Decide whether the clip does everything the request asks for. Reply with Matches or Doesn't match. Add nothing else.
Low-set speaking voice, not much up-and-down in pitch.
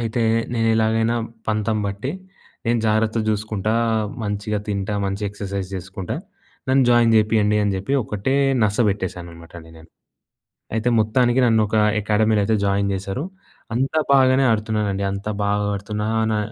Matches